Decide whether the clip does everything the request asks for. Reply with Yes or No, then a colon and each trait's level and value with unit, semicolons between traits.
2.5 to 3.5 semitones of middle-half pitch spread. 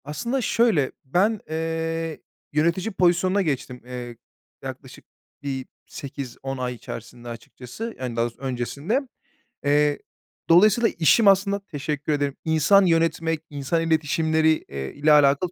No: average, 4.8 semitones